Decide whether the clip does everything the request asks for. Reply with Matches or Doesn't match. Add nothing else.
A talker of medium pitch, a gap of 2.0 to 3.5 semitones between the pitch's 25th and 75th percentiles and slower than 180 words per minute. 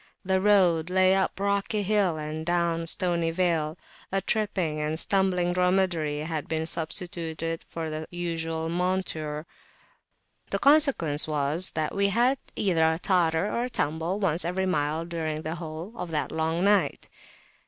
Matches